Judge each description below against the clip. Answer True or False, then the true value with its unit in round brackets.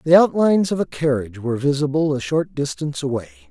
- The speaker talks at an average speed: True (190 wpm)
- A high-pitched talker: False (150 Hz)